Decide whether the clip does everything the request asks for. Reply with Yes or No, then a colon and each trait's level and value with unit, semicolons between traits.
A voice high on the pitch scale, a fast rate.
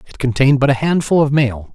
No: low, 135 Hz; fast, 240 wpm